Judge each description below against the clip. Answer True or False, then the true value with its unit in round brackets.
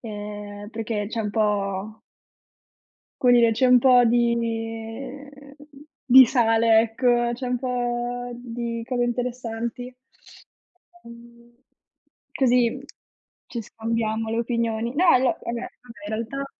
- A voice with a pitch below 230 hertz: False (235 Hz)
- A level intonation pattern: True (1.7 semitones)